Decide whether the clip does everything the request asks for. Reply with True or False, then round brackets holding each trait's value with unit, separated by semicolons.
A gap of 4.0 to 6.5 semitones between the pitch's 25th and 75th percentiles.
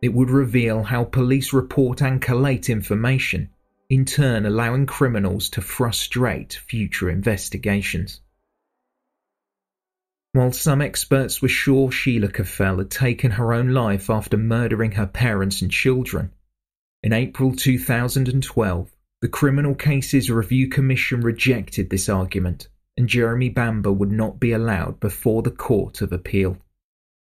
True (4.6 semitones)